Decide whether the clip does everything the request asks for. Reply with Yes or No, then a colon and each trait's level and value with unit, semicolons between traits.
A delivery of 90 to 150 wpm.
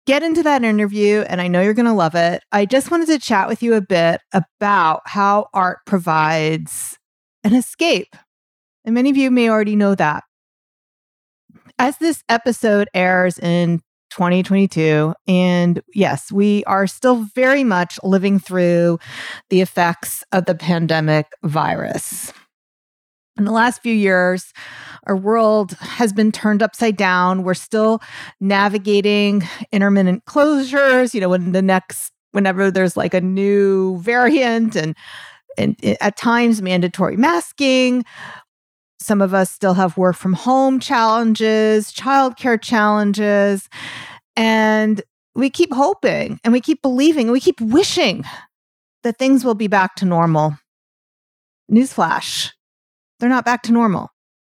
Yes: average, 140 wpm